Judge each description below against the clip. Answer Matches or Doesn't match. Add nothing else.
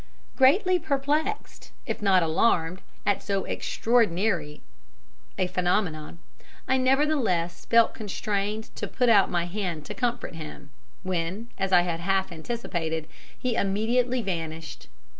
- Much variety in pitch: Matches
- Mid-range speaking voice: Doesn't match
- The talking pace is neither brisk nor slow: Doesn't match